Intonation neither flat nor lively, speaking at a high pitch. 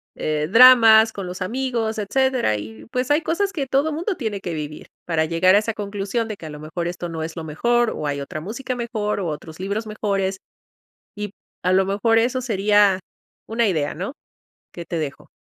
No: wide, 5.8 semitones; high, 205 Hz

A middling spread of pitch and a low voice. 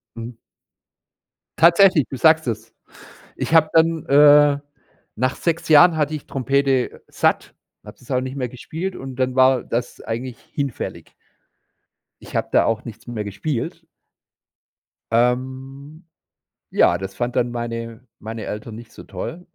Yes: average, 4.1 semitones; low, 130 Hz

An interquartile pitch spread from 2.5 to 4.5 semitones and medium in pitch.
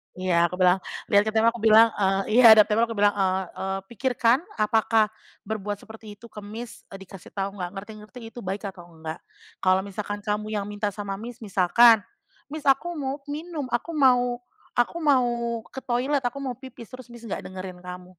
No: average, 3.8 semitones; high, 215 Hz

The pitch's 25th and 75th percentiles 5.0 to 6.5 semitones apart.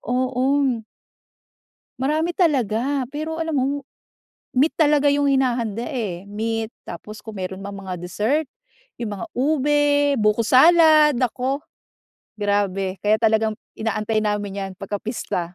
Yes: wide, 5.6 semitones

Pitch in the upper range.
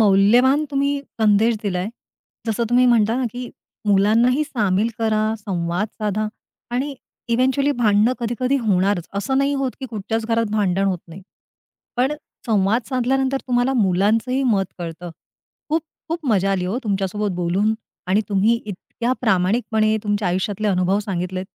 Yes: high, 215 Hz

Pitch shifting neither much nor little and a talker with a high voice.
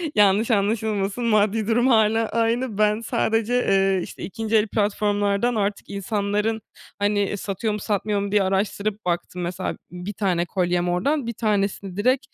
No: narrow, 2.2 semitones; high, 205 Hz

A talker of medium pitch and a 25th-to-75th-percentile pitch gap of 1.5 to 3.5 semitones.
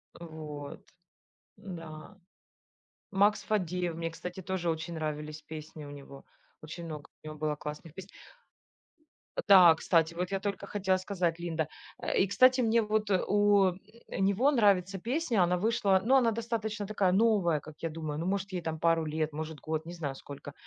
No: medium, 175 Hz; average, 4.2 semitones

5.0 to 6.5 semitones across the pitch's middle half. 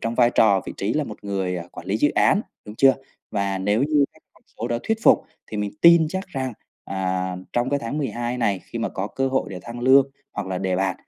Yes: wide, 5.6 semitones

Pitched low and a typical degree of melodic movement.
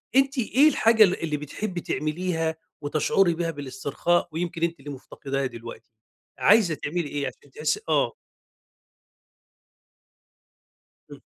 No: medium, 160 Hz; average, 3.8 semitones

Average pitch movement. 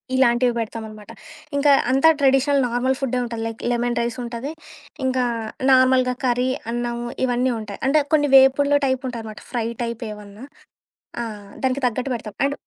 No: narrow, 2.2 semitones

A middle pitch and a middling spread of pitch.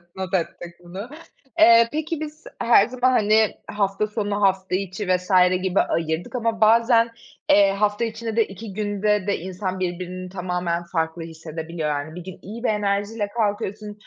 No: high, 200 Hz; average, 3.3 semitones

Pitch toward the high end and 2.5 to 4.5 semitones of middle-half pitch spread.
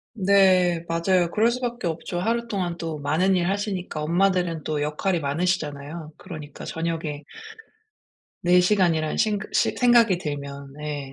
No: medium, 175 Hz; average, 4.0 semitones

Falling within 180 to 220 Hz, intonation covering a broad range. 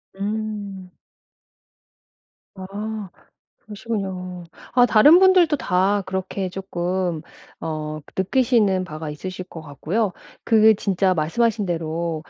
No: high, 190 Hz; average, 3.6 semitones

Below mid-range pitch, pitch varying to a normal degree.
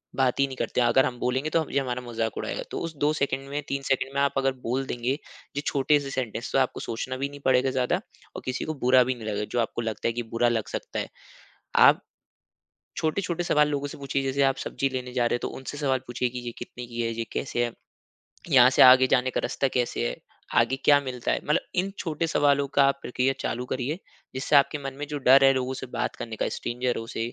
No: low, 130 Hz; narrow, 2.2 semitones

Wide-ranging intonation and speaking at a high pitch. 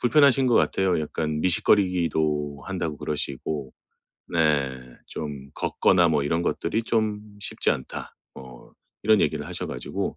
No: wide, 5.7 semitones; very low, 80 Hz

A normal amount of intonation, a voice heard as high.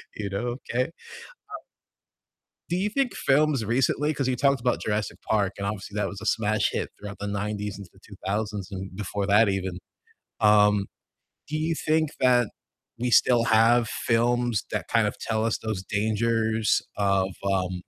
No: average, 3.3 semitones; low, 110 Hz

